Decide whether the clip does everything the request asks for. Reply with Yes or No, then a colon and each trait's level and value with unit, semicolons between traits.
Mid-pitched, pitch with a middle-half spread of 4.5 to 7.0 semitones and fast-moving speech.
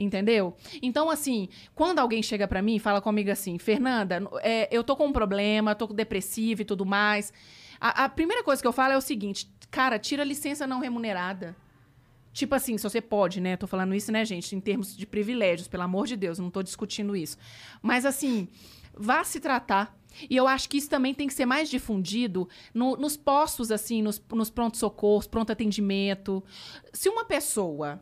No: high, 215 Hz; average, 4.8 semitones; fast, 195 wpm